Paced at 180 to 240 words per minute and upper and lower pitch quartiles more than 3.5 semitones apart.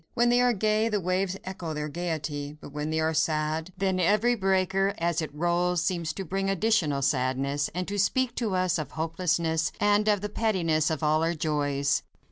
Yes: average, 195 wpm; average, 4.0 semitones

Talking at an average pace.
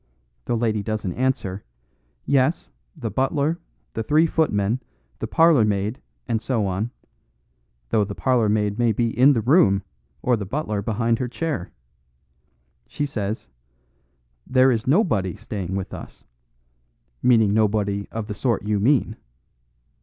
No: slow, 130 wpm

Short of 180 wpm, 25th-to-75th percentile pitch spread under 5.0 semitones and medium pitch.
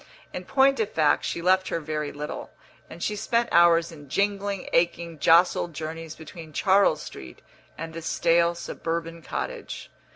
Yes: average, 155 wpm; average, 2.8 semitones; medium, 170 Hz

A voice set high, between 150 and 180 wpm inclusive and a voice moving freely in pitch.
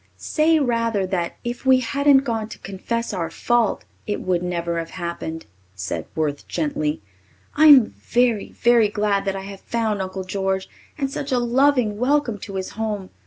No: high, 210 Hz; average, 165 wpm; average, 4.6 semitones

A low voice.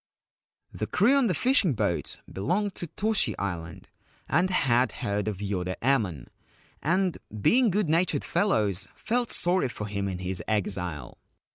Yes: low, 120 Hz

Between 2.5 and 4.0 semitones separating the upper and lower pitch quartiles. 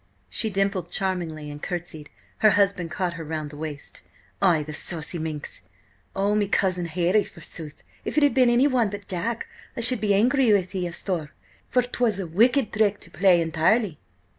No: average, 4.7 semitones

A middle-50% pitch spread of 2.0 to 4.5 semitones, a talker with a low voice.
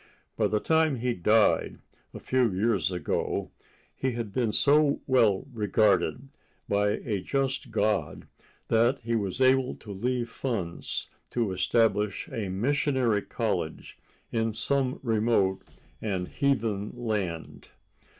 Yes: average, 4.0 semitones; low, 115 Hz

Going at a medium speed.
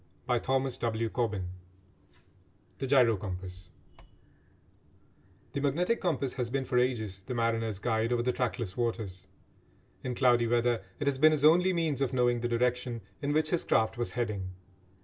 Yes: average, 150 wpm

